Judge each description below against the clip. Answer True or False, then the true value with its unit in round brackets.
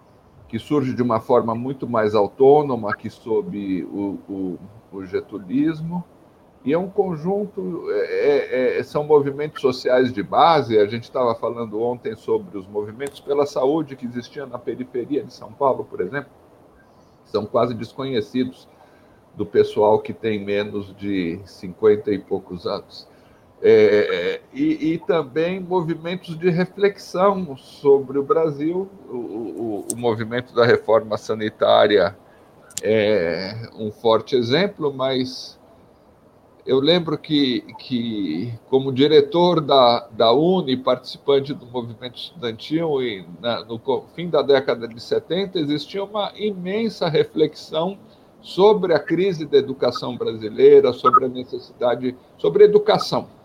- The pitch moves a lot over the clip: True (8.8 semitones)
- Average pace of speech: False (130 wpm)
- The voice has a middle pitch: True (150 Hz)